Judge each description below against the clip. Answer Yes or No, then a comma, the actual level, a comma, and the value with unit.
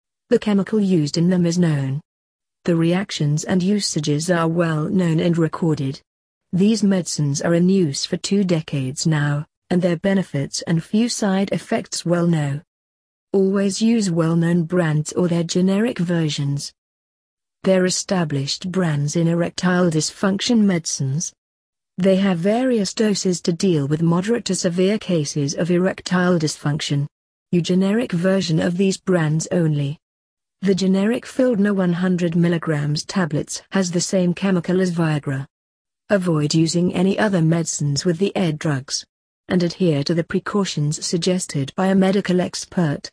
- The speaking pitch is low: No, medium, 175 Hz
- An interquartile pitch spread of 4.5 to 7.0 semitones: No, average, 3.5 semitones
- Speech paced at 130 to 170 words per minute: Yes, average, 140 wpm